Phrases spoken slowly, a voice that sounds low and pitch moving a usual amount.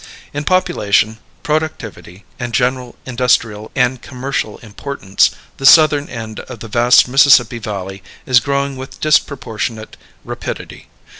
Yes: slow, 120 wpm; low, 125 Hz; average, 4.0 semitones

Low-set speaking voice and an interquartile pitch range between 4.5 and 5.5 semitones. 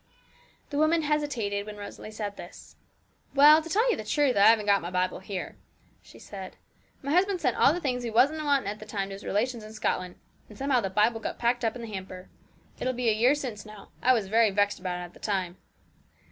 No: high, 220 Hz; average, 5.0 semitones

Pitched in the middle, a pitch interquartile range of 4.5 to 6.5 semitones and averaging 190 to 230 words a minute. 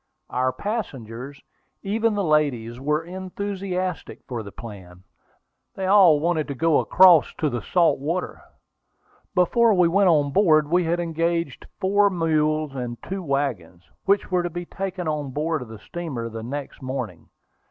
No: medium, 160 Hz; wide, 5.6 semitones; average, 155 wpm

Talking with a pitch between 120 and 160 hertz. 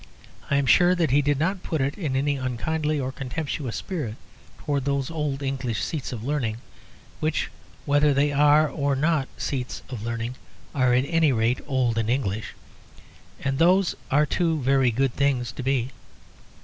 Yes: medium, 140 Hz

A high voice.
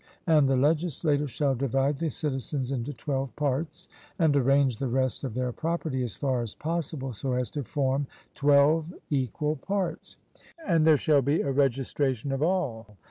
No: medium, 140 Hz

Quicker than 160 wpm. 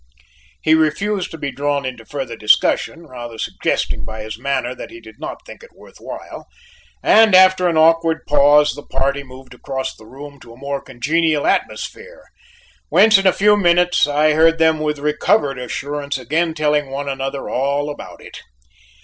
Yes: average, 175 wpm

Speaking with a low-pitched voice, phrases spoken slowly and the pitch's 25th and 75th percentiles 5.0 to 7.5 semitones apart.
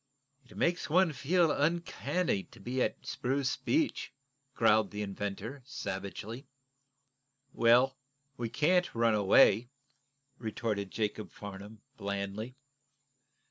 Yes: low, 115 Hz; slow, 100 wpm; wide, 5.5 semitones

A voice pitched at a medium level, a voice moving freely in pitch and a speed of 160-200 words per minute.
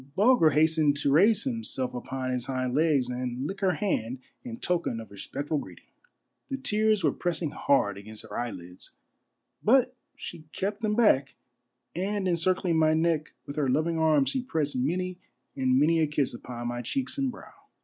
Yes: medium, 155 Hz; wide, 6.5 semitones; average, 170 wpm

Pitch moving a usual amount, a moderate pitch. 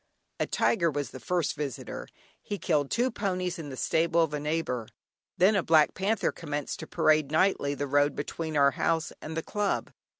Yes: average, 3.8 semitones; medium, 160 Hz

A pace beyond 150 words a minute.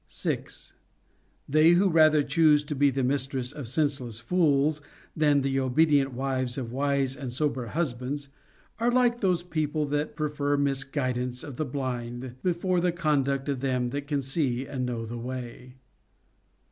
Yes: average, 160 wpm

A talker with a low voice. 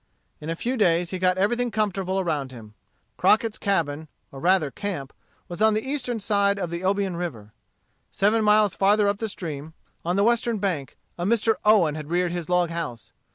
No: medium, 185 Hz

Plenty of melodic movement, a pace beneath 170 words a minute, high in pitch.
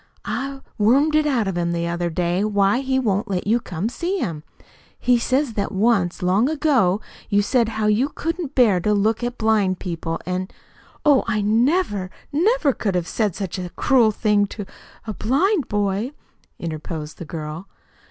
No: wide, 5.9 semitones; average, 185 wpm; high, 210 Hz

